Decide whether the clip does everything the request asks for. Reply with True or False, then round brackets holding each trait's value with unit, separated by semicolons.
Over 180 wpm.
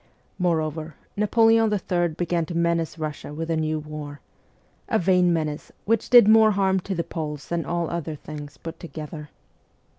False (160 wpm)